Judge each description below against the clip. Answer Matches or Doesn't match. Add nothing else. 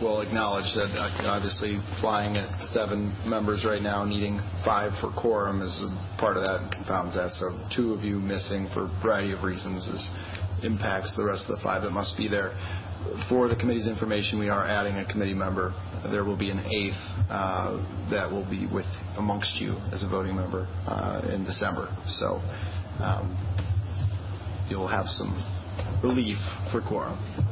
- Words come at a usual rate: Matches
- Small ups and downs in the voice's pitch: Matches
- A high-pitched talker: Doesn't match